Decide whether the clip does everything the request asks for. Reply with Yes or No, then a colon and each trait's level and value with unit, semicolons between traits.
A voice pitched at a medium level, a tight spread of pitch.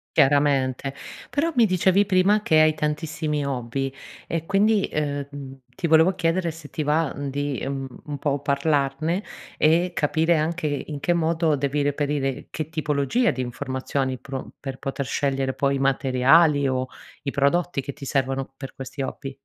No: medium, 145 Hz; average, 3.0 semitones